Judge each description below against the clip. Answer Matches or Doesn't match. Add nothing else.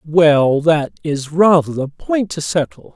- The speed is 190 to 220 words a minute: Doesn't match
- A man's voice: Matches